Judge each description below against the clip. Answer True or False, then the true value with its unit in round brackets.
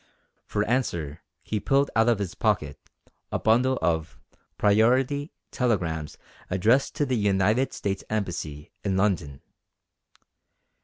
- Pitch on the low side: True (105 Hz)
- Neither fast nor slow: False (115 wpm)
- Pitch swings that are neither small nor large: False (5.9 semitones)